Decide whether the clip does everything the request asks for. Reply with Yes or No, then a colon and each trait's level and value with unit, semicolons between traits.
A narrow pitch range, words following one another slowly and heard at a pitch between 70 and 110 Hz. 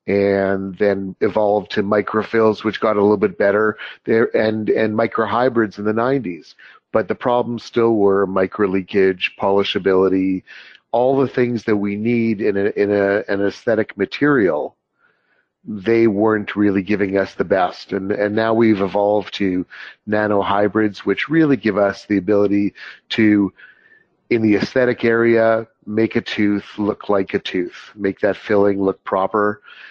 No: narrow, 2.2 semitones; average, 150 wpm; low, 105 Hz